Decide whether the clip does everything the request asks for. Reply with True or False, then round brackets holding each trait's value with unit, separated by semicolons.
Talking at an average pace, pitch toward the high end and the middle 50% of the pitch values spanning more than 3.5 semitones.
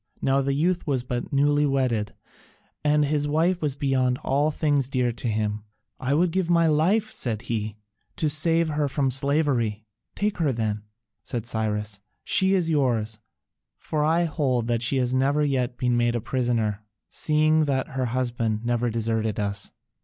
False (170 wpm; 130 Hz; 4.4 semitones)